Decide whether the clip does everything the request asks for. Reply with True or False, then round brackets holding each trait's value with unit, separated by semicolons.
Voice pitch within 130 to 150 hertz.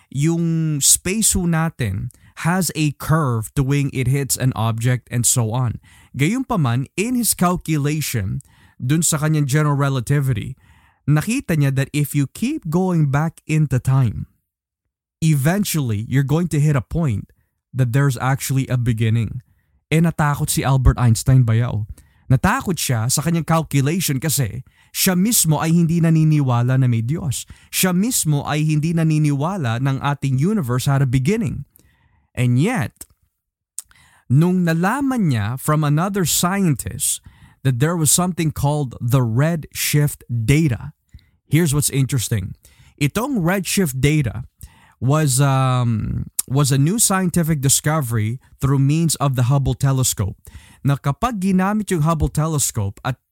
True (140 Hz)